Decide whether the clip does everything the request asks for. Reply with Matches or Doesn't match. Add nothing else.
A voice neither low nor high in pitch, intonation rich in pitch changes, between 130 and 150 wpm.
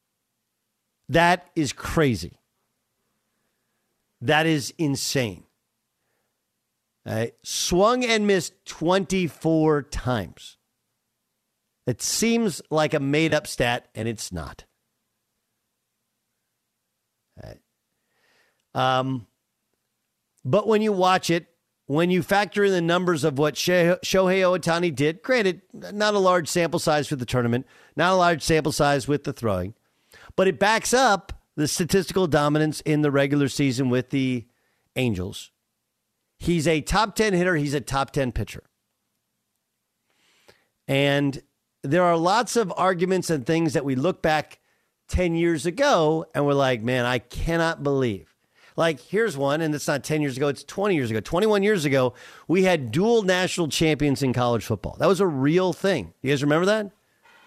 Matches